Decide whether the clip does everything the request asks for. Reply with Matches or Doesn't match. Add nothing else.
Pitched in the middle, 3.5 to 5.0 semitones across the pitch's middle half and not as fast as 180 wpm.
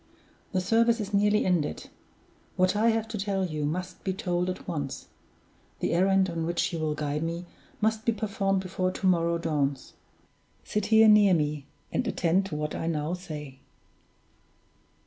Matches